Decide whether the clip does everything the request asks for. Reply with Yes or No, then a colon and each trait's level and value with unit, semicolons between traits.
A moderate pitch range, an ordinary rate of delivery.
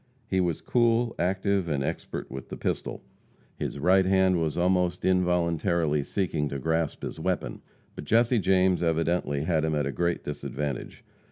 Yes: average, 3.4 semitones; average, 160 wpm